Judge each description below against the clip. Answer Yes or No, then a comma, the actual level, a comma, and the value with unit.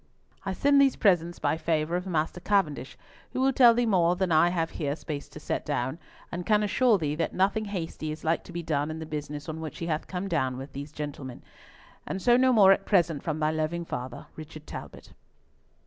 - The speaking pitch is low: No, medium, 165 Hz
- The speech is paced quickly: Yes, fast, 220 wpm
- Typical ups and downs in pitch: Yes, average, 4.0 semitones